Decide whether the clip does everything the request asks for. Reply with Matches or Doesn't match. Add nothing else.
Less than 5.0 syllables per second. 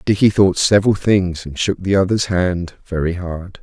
Matches